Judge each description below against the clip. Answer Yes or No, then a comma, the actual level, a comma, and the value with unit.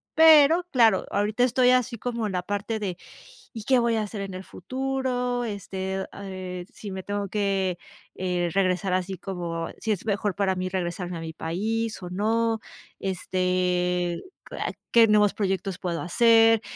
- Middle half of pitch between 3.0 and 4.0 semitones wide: Yes, average, 3.7 semitones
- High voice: Yes, high, 200 Hz